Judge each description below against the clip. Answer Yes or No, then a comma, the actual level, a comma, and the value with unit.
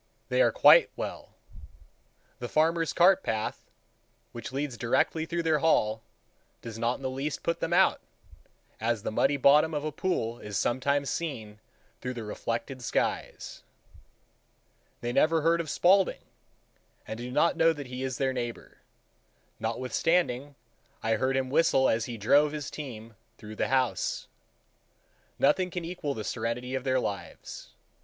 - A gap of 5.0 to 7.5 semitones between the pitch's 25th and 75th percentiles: Yes, average, 5.3 semitones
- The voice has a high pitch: No, low, 130 Hz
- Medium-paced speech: Yes, average, 150 wpm